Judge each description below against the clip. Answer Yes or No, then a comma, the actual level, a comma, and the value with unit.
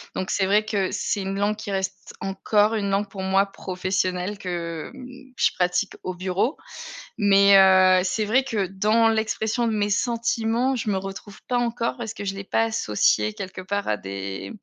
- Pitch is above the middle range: Yes, high, 200 Hz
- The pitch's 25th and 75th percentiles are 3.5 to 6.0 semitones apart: No, average, 2.8 semitones